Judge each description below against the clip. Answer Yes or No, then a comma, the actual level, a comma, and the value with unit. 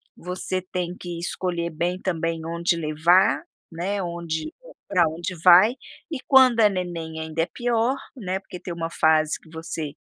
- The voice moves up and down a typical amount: No, narrow, 2.2 semitones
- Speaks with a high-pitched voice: No, medium, 175 Hz